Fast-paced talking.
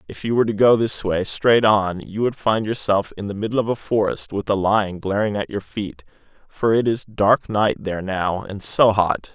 Yes: fast, 230 wpm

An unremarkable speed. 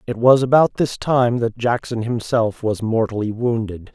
Yes: average, 165 wpm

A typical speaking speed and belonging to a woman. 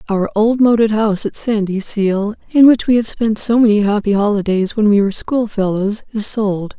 Yes: average, 185 wpm; female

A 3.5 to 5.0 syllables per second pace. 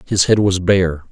Yes: 4.2 syllables/s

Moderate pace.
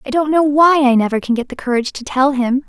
No: fast, 290 wpm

